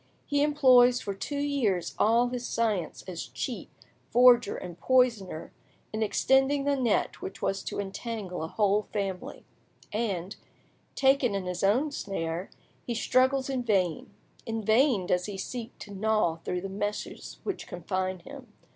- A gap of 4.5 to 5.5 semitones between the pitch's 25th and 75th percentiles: Yes, average, 4.9 semitones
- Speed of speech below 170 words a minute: Yes, average, 150 wpm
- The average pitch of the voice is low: No, high, 215 Hz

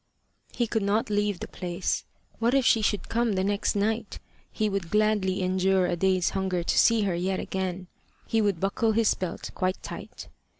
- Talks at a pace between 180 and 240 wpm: Yes, average, 185 wpm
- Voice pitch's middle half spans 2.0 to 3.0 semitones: Yes, narrow, 2.6 semitones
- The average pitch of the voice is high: Yes, high, 195 Hz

